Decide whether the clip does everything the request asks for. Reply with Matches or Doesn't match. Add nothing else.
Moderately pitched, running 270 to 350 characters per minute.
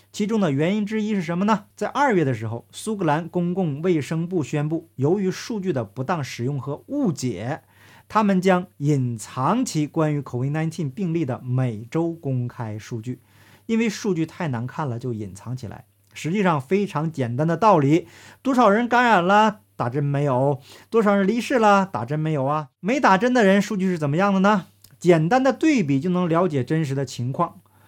Matches